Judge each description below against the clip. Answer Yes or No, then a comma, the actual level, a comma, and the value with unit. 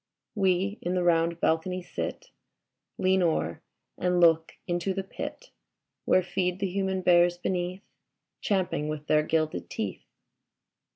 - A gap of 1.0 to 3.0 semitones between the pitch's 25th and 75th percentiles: Yes, narrow, 2.4 semitones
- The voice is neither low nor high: Yes, medium, 180 Hz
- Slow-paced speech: Yes, slow, 130 wpm